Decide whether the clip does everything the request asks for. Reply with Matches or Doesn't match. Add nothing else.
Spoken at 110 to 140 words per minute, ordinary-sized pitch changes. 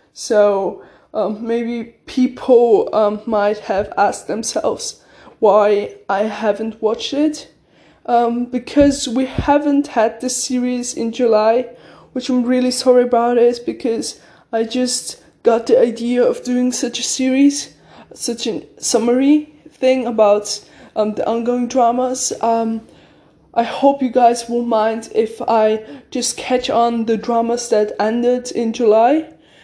Doesn't match